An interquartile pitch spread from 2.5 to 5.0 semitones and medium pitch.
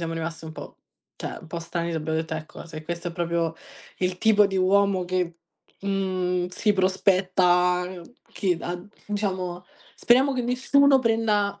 Yes: average, 2.8 semitones; medium, 180 Hz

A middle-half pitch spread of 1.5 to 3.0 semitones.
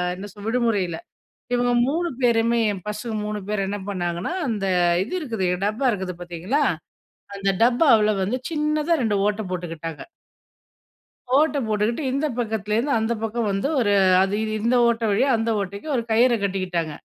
No: average, 3.7 semitones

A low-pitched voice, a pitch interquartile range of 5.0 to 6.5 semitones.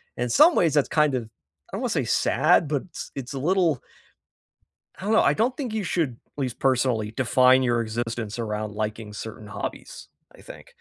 Yes: low, 125 Hz; wide, 5.6 semitones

